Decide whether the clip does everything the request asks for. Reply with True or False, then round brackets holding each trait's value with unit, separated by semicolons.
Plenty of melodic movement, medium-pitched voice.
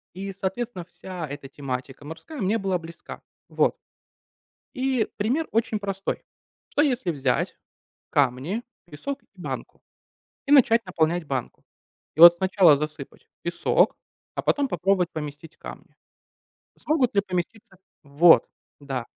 True (6.8 semitones; 180 Hz)